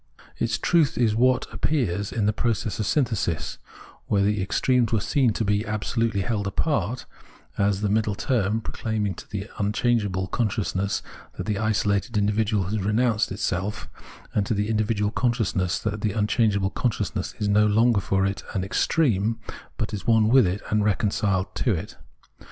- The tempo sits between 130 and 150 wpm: No, average, 175 wpm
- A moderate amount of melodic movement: No, narrow, 2.2 semitones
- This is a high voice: No, low, 105 Hz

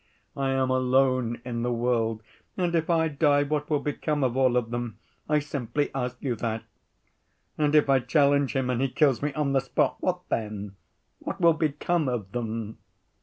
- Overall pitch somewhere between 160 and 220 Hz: No, low, 135 Hz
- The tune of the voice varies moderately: Yes, average, 3.5 semitones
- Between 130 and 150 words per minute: No, average, 185 wpm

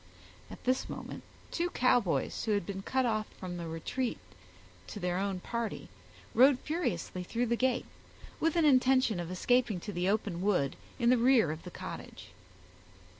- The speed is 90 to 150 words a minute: No, average, 170 wpm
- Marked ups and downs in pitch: Yes, wide, 5.8 semitones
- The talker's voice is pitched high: Yes, high, 220 Hz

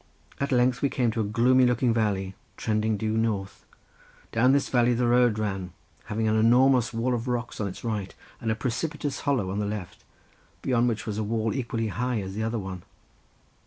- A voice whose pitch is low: Yes, low, 115 Hz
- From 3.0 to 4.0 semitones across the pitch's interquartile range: No, narrow, 2.6 semitones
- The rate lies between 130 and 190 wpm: No, average, 200 wpm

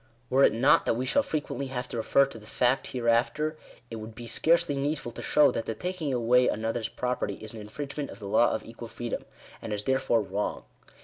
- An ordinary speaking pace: No, fast, 220 wpm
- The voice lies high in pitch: No, low, 125 Hz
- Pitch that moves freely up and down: No, average, 3.6 semitones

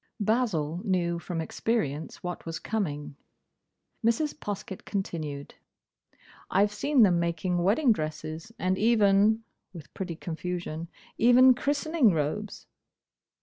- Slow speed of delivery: Yes, slow, 105 wpm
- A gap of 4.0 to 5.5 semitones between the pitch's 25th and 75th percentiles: Yes, average, 5.2 semitones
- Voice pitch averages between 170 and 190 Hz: Yes, medium, 185 Hz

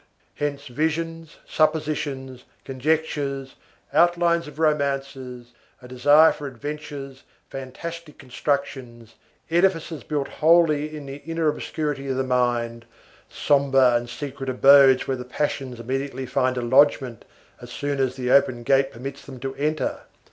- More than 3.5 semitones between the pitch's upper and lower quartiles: No, average, 2.8 semitones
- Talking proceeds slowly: Yes, slow, 130 wpm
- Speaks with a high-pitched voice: No, medium, 140 Hz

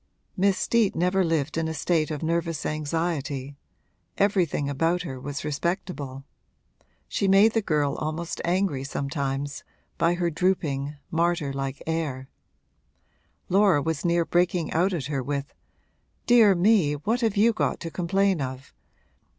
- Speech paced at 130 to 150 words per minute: Yes, average, 140 wpm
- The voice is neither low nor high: Yes, medium, 165 Hz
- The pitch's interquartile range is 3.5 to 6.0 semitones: Yes, average, 4.3 semitones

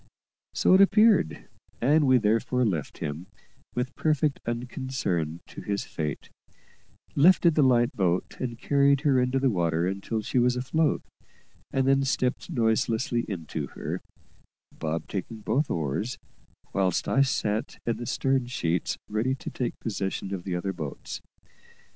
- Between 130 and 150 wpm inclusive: Yes, average, 145 wpm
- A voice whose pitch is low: Yes, low, 120 Hz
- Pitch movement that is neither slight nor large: No, wide, 5.8 semitones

